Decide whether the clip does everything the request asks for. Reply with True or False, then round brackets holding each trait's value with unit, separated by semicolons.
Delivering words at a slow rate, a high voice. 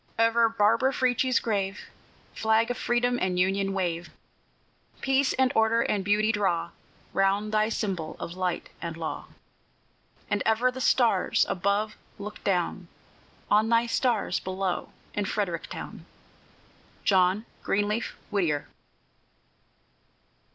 True (115 wpm; 205 Hz)